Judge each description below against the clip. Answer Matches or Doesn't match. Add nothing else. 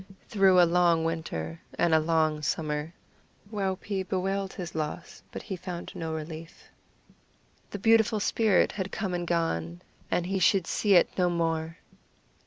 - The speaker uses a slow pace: Doesn't match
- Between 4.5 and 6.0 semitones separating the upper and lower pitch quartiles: Doesn't match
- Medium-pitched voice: Matches